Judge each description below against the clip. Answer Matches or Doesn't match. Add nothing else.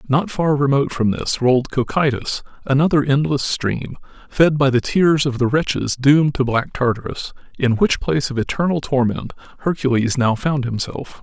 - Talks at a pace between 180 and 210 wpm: Doesn't match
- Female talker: Doesn't match